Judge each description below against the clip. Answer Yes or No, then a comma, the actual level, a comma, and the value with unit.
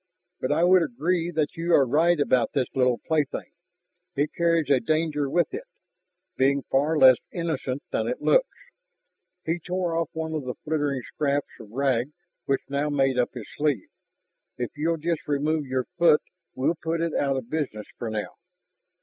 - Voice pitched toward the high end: No, medium, 145 Hz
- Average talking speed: Yes, average, 175 wpm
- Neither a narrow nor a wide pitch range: Yes, average, 3.8 semitones